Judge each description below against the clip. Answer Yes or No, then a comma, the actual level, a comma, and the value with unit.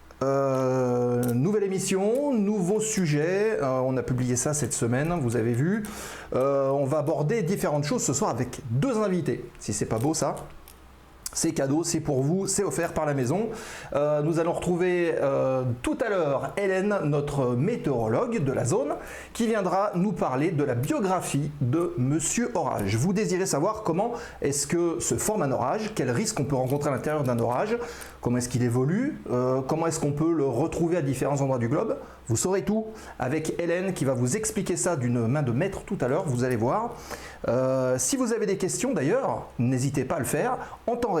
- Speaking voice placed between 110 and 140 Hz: No, medium, 150 Hz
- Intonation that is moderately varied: No, wide, 6.6 semitones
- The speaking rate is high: No, average, 195 wpm